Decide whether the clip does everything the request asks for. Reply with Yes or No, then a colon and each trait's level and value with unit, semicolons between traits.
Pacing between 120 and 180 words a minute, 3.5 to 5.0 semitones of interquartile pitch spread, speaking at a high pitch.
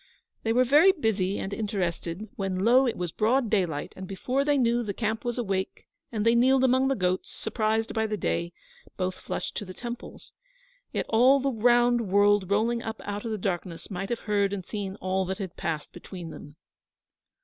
No: average, 195 wpm; average, 4.0 semitones; high, 210 Hz